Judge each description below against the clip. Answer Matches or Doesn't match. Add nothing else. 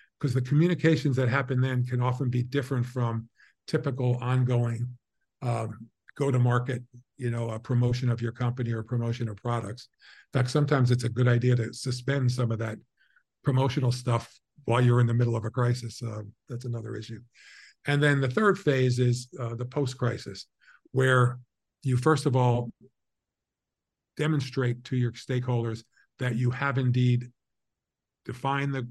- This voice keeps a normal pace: Matches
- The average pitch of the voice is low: Matches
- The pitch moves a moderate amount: Doesn't match